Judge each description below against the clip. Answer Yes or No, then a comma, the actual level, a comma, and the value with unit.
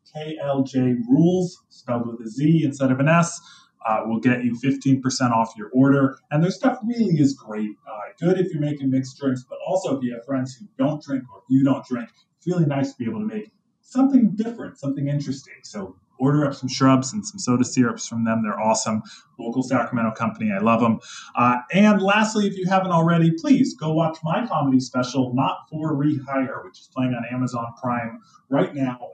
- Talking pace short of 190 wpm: No, fast, 205 wpm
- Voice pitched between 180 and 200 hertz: No, low, 135 Hz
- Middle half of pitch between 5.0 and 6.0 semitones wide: Yes, average, 5.3 semitones